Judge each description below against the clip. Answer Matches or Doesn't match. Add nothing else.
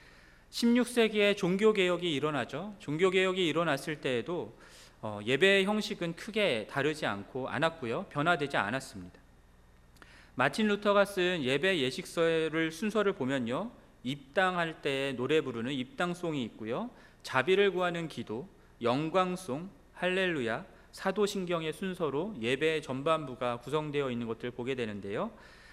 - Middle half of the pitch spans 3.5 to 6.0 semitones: Doesn't match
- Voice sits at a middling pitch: Matches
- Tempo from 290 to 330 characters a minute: Matches